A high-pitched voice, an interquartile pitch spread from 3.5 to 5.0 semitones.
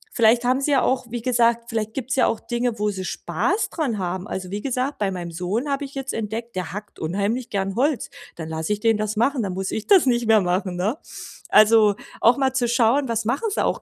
Yes: high, 225 Hz; average, 4.1 semitones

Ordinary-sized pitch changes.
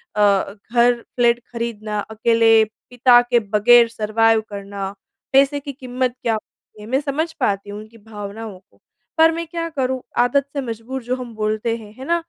Yes: average, 3.2 semitones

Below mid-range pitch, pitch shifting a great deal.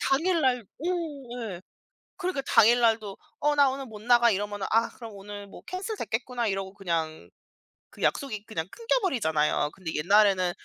No: high, 225 Hz; wide, 5.8 semitones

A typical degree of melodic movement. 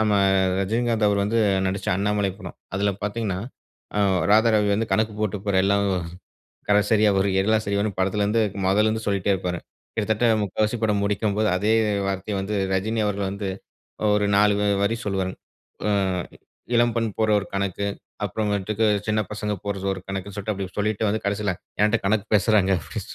No: narrow, 1.6 semitones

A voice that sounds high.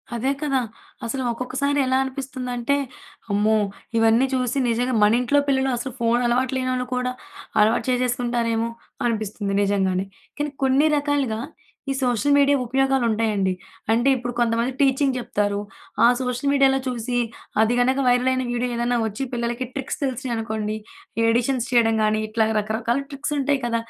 Yes: high, 245 Hz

